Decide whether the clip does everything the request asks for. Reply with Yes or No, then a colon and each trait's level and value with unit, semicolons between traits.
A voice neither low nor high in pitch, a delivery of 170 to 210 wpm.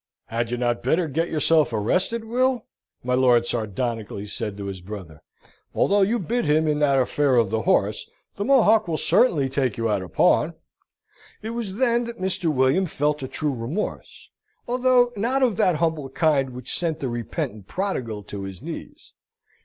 Yes: medium, 145 Hz; average, 175 wpm